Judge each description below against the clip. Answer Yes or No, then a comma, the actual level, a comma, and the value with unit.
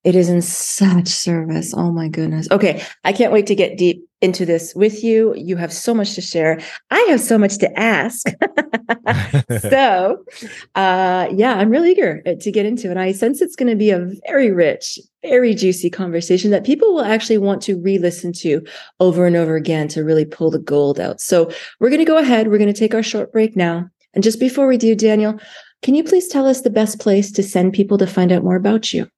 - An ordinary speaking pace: No, fast, 220 wpm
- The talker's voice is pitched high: Yes, high, 200 Hz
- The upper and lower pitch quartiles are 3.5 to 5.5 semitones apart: Yes, average, 4.5 semitones